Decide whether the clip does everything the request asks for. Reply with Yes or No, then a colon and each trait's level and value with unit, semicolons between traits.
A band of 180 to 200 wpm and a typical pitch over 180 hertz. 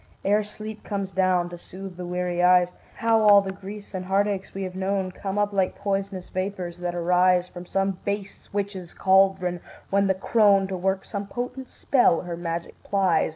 Yes: average, 185 wpm; high, 190 Hz